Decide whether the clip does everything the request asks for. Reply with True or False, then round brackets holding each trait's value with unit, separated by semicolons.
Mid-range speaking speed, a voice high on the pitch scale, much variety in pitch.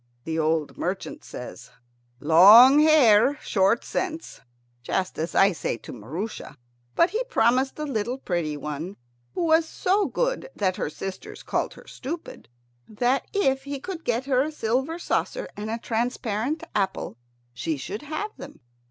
True (150 wpm; 235 Hz; 8.3 semitones)